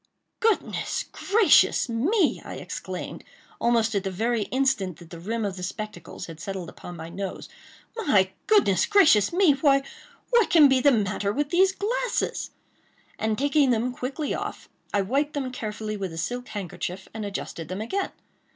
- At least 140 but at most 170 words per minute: Yes, average, 160 wpm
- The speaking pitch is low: No, high, 230 Hz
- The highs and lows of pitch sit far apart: Yes, wide, 6.9 semitones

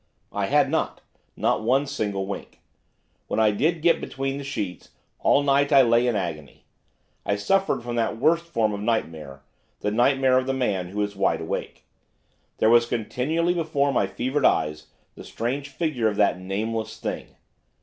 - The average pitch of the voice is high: No, low, 120 Hz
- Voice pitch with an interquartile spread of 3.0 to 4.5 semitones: No, average, 5.3 semitones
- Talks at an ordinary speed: Yes, average, 170 wpm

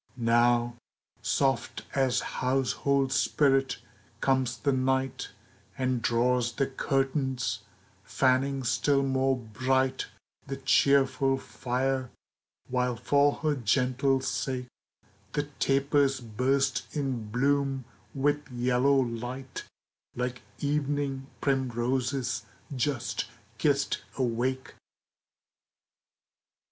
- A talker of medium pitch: No, low, 130 Hz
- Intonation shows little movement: Yes, narrow, 1.6 semitones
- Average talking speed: No, slow, 85 wpm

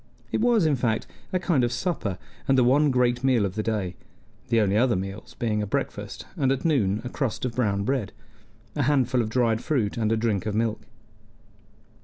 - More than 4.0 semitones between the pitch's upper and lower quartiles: No, average, 3.7 semitones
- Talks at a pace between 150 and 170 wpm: No, average, 200 wpm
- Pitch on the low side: Yes, low, 120 Hz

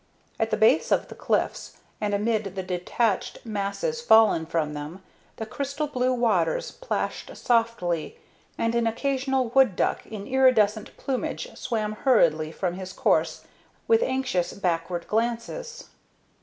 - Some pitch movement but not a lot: No, wide, 5.7 semitones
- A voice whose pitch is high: Yes, high, 220 Hz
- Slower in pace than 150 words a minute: Yes, slow, 135 wpm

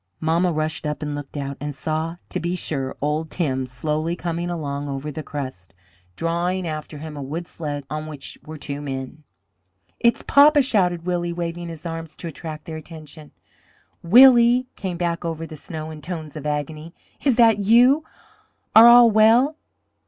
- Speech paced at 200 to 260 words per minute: No, average, 170 wpm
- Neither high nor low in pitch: Yes, medium, 160 Hz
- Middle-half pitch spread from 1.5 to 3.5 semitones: Yes, average, 3.0 semitones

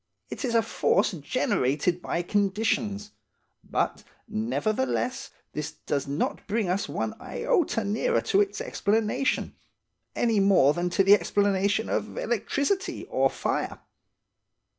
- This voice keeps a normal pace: No, slow, 120 wpm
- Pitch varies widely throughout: No, average, 3.7 semitones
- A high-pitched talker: Yes, high, 210 Hz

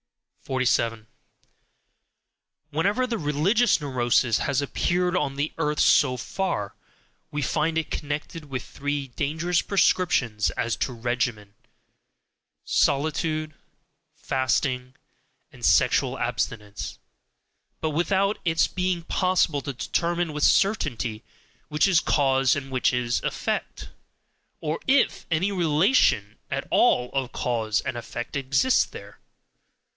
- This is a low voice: No, medium, 145 Hz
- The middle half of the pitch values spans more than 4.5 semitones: Yes, wide, 5.5 semitones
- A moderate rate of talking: No, slow, 110 wpm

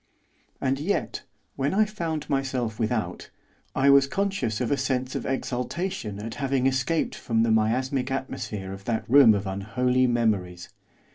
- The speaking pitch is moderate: No, low, 130 Hz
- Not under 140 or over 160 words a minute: Yes, average, 150 wpm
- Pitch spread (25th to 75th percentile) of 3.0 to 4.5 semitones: Yes, average, 3.7 semitones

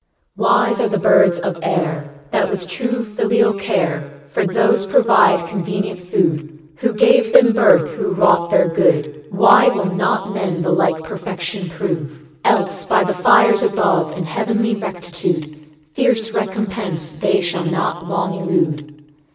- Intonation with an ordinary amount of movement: Yes, average, 3.9 semitones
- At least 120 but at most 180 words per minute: Yes, average, 150 wpm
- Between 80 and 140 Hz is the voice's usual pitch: No, medium, 180 Hz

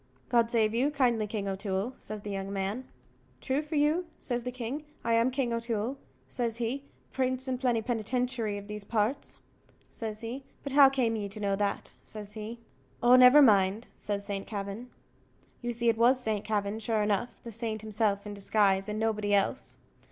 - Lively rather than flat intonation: No, average, 3.3 semitones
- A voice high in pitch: Yes, high, 225 Hz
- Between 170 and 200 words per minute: Yes, average, 180 wpm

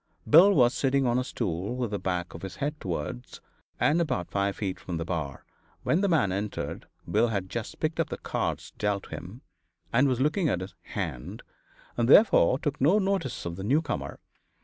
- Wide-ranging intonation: Yes, wide, 7.8 semitones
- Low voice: Yes, low, 115 Hz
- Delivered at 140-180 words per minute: No, average, 195 wpm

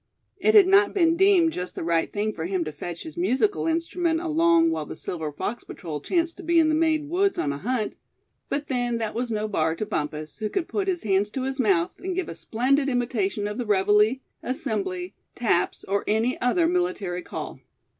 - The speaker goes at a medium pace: No, fast, 210 wpm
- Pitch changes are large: Yes, wide, 9.0 semitones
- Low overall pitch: No, high, 245 Hz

